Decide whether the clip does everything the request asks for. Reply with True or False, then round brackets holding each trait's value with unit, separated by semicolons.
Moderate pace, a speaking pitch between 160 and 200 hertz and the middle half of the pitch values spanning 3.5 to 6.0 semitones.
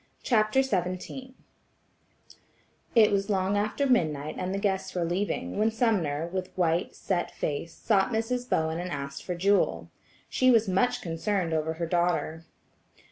True (145 wpm; 185 Hz; 4.4 semitones)